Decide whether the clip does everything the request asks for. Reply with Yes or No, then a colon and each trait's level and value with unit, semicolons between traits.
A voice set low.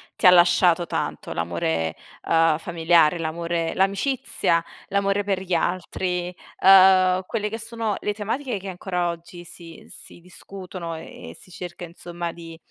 No: medium, 175 Hz